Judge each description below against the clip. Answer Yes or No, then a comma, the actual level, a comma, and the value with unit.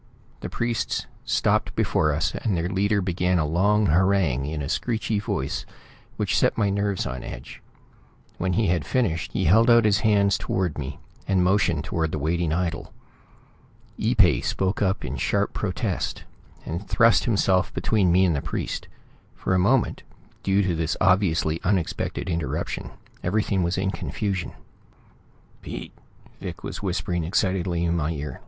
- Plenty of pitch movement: No, average, 3.5 semitones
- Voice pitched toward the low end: Yes, very low, 90 Hz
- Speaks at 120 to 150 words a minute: No, average, 160 wpm